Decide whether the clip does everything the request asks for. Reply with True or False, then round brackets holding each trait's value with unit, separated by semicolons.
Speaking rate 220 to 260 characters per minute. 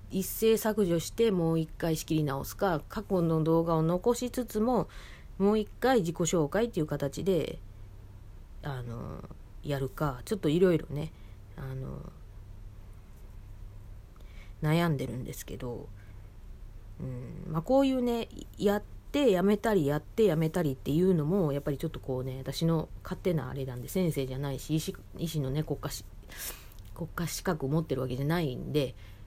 False (305 characters per minute)